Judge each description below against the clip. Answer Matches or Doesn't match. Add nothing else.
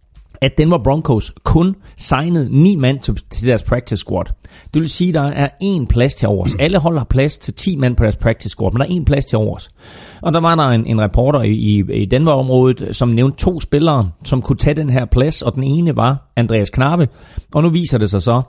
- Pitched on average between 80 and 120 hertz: Doesn't match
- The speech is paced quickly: Matches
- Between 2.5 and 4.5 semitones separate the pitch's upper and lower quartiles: Doesn't match